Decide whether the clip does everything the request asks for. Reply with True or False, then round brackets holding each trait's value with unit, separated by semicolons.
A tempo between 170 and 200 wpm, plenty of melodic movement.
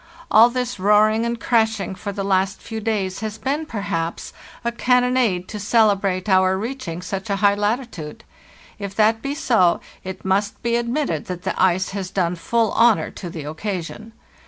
False (175 wpm; 3.5 semitones)